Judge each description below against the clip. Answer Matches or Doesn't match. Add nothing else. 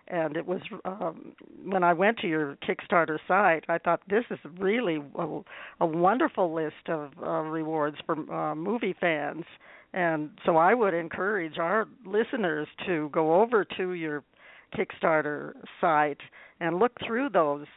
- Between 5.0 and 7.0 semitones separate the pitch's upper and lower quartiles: Doesn't match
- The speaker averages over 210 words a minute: Doesn't match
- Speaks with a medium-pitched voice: Matches